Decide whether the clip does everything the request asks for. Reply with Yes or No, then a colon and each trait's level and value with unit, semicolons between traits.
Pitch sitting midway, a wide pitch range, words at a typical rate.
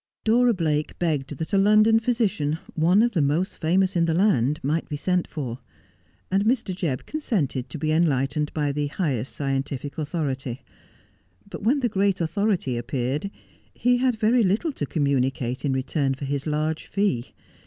Yes: medium, 155 Hz; wide, 6.3 semitones; average, 165 wpm